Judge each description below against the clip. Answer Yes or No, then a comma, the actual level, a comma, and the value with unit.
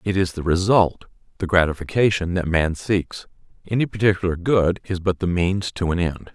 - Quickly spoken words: No, average, 180 wpm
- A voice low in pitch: Yes, very low, 90 Hz